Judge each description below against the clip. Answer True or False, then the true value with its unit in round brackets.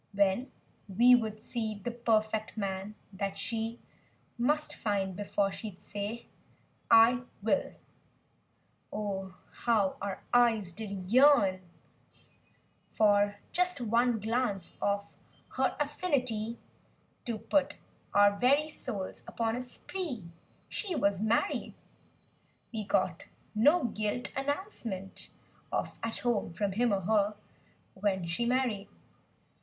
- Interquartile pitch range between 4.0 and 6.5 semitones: False (3.4 semitones)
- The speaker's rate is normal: False (115 wpm)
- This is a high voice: True (220 Hz)